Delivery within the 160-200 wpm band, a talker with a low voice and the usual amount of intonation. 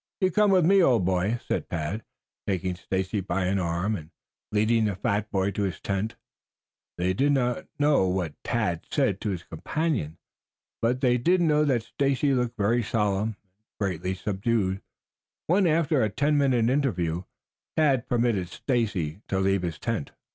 No: average, 165 wpm; low, 110 Hz; wide, 5.8 semitones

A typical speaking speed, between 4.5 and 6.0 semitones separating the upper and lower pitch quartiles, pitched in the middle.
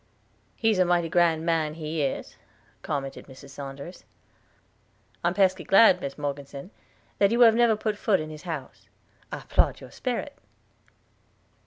Yes: average, 150 wpm; average, 5.3 semitones; medium, 165 Hz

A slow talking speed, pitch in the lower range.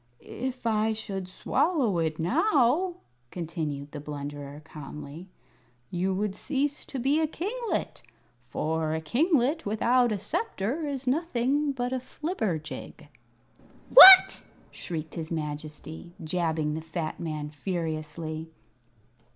No: slow, 115 wpm; high, 190 Hz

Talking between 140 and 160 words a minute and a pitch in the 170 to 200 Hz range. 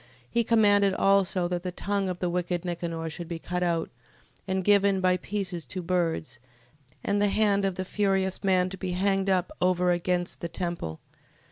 No: average, 180 wpm; medium, 185 Hz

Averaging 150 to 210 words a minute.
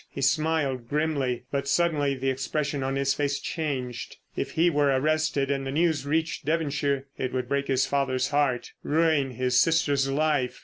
Yes: average, 170 wpm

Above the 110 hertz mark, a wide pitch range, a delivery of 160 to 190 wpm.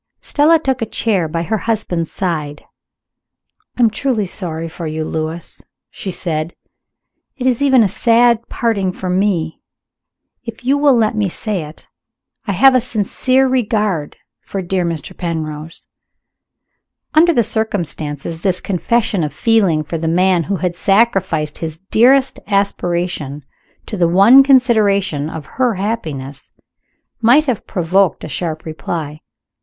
No: high, 190 Hz; wide, 6.0 semitones; average, 140 wpm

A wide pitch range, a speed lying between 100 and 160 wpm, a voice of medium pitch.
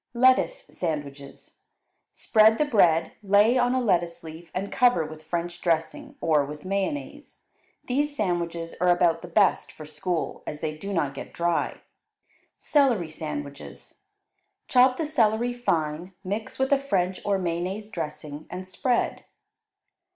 Yes: wide, 6.2 semitones; average, 140 wpm; medium, 180 Hz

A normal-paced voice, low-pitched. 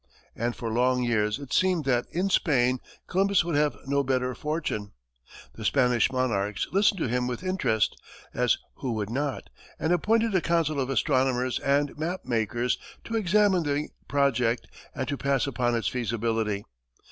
Yes: average, 160 wpm; low, 130 Hz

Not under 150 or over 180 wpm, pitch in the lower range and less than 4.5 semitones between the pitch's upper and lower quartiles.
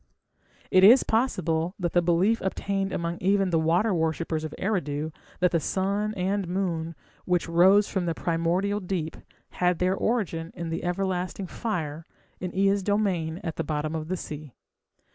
No: average, 160 wpm; medium, 180 Hz; average, 3.1 semitones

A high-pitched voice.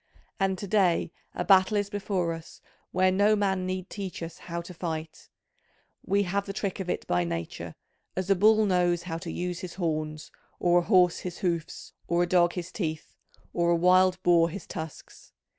No: medium, 180 Hz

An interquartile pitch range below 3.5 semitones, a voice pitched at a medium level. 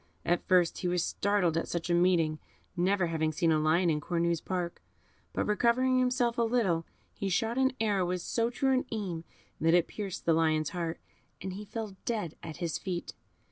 No: average, 4.6 semitones; medium, 180 Hz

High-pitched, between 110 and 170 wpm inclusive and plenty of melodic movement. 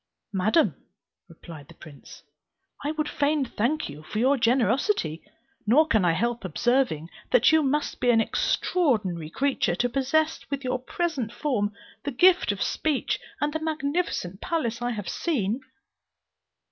Yes: very high, 250 Hz; average, 145 wpm; wide, 6.5 semitones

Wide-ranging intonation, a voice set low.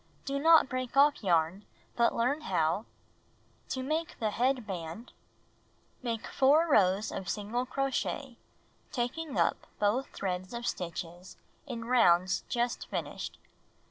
No: wide, 6.1 semitones; high, 235 Hz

